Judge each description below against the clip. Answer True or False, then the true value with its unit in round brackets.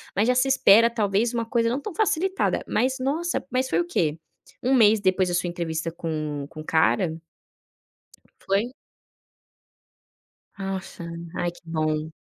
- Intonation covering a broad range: True (7.2 semitones)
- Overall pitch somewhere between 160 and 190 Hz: False (200 Hz)